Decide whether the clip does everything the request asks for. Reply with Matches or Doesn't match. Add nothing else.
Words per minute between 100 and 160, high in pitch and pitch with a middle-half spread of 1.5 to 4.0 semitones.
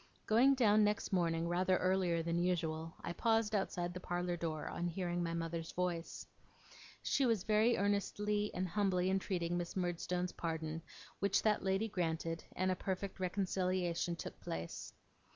Doesn't match